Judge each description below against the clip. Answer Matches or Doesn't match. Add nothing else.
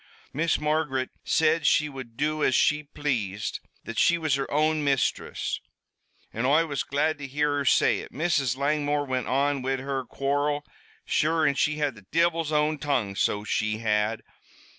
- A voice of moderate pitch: Matches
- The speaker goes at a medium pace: Matches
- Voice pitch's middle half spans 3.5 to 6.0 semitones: Doesn't match